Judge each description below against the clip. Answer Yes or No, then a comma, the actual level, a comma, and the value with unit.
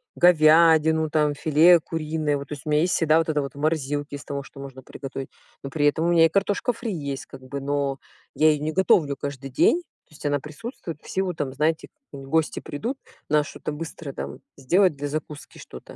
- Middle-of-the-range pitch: Yes, medium, 150 Hz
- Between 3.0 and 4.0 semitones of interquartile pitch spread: No, narrow, 2.4 semitones